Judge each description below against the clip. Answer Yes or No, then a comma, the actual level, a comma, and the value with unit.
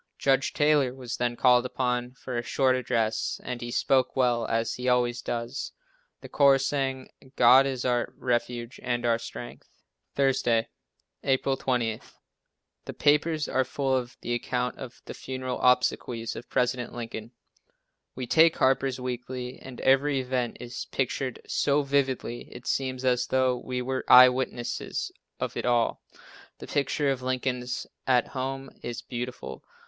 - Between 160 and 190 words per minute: No, average, 150 wpm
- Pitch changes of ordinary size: No, narrow, 1.6 semitones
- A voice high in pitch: No, low, 125 Hz